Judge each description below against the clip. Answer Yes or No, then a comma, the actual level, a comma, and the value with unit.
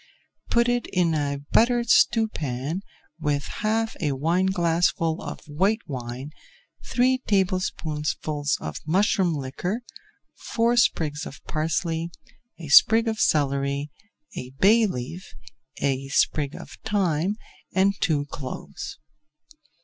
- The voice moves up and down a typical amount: No, wide, 6.4 semitones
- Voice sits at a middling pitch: Yes, medium, 165 Hz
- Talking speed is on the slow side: Yes, slow, 110 wpm